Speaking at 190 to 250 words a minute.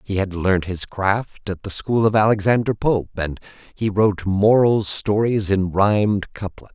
No: average, 170 wpm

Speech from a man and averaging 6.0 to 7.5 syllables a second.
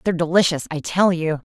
No: female; 6.2 syllables/s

